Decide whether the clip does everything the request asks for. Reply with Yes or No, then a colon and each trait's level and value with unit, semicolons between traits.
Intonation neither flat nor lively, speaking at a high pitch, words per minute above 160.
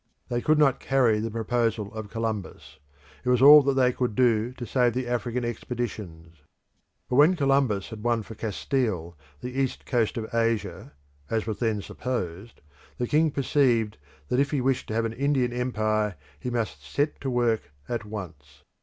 No: average, 3.1 semitones; low, 120 Hz; average, 175 wpm